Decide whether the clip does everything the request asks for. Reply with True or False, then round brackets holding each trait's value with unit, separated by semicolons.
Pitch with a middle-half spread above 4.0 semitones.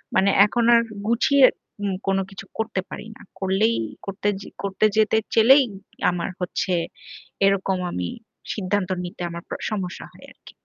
False (2.7 semitones)